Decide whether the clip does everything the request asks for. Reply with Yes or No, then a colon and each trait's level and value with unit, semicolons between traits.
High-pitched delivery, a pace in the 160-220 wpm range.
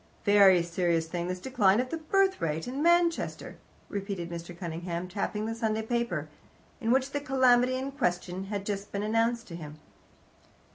Yes: high, 205 Hz; average, 170 wpm